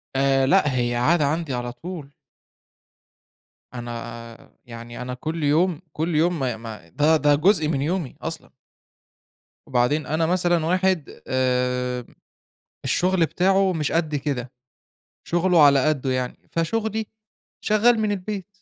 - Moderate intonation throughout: No, wide, 5.8 semitones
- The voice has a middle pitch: Yes, medium, 150 Hz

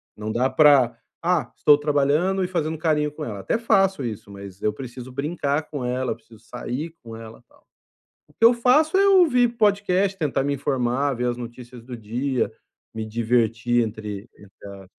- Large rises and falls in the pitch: Yes, wide, 5.8 semitones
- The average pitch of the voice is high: No, low, 130 Hz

